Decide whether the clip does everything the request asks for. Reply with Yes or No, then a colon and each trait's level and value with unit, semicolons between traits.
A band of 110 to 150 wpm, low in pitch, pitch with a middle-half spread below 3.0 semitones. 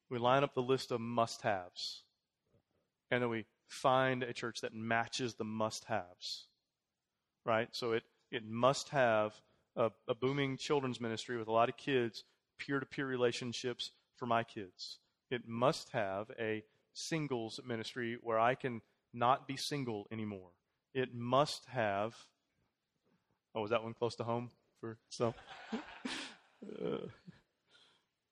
Yes: average, 145 wpm; low, 120 Hz; narrow, 2.4 semitones